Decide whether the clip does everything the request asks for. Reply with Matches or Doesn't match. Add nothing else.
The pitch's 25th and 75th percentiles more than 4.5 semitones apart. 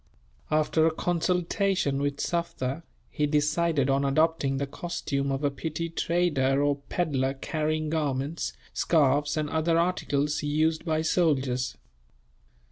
Doesn't match